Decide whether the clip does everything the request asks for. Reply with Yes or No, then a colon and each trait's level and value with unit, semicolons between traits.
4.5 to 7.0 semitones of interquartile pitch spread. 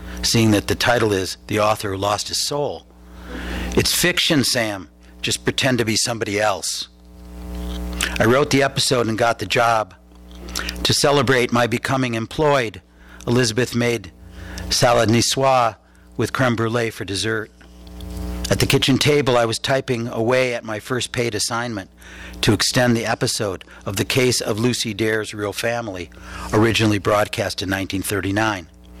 Yes: average, 5.3 semitones